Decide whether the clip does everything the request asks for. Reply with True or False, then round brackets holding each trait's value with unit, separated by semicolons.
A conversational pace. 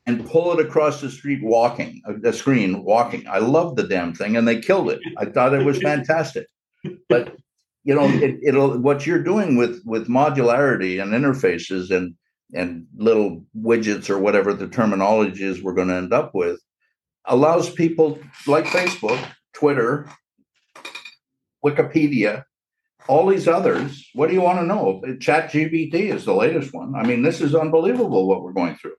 True (170 wpm)